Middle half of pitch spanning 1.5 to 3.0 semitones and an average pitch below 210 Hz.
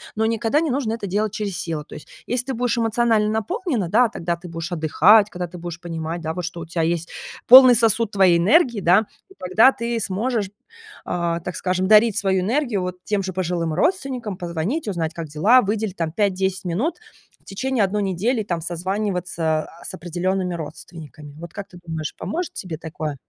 No: average, 4.8 semitones; high, 190 Hz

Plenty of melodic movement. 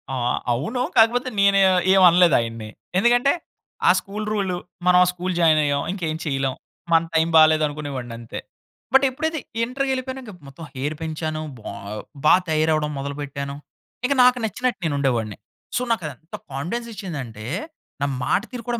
Yes: wide, 8.0 semitones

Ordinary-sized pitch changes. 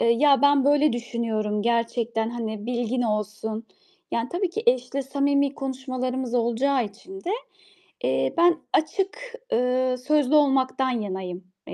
Yes: average, 3.4 semitones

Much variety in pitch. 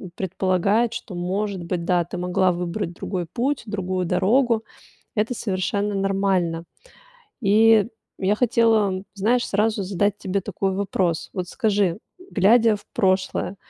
No: average, 2.7 semitones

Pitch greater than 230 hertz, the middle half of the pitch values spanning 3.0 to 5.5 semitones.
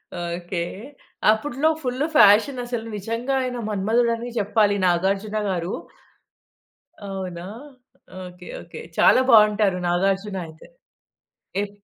No: high, 205 Hz; average, 4.1 semitones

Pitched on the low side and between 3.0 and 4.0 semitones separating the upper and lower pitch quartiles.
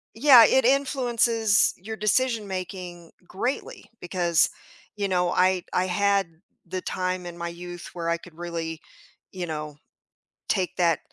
No: medium, 185 Hz; average, 3.7 semitones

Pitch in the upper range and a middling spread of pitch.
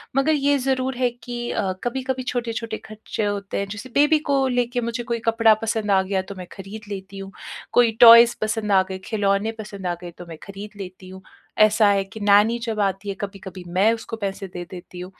Yes: high, 210 Hz; average, 3.4 semitones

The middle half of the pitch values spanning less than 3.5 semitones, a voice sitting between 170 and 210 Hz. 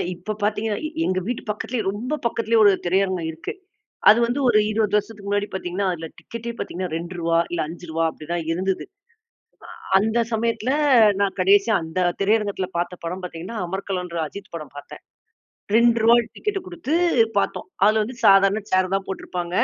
No: average, 3.8 semitones; high, 195 Hz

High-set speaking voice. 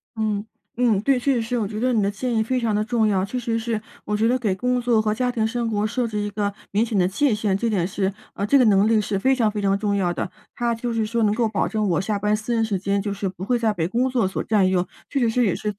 Yes: high, 215 Hz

